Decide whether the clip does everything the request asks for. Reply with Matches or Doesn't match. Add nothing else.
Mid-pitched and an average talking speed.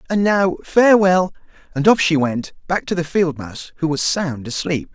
Matches